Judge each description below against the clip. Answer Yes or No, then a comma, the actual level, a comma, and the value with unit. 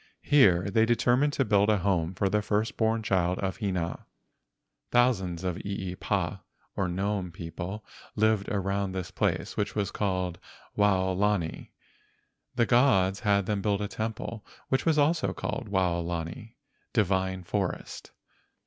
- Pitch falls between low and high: No, low, 100 Hz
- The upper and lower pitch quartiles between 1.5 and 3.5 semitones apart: Yes, average, 2.9 semitones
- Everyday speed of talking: No, slow, 130 wpm